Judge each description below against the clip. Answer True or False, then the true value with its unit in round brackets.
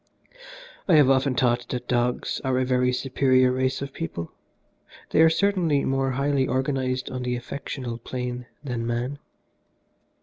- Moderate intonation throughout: False (1.6 semitones)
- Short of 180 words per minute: True (145 wpm)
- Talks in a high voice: False (130 Hz)